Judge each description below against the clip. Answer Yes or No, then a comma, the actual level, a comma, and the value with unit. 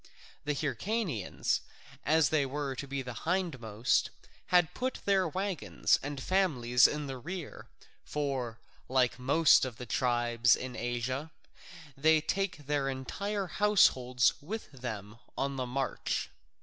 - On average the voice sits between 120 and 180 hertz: Yes, medium, 140 Hz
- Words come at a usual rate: No, slow, 130 wpm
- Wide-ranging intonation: No, average, 4.7 semitones